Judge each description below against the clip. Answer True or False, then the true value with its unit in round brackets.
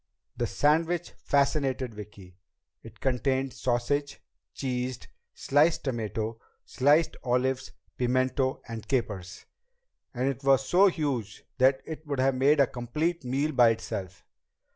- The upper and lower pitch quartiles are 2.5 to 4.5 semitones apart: True (3.0 semitones)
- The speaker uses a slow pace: True (120 wpm)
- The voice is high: False (130 Hz)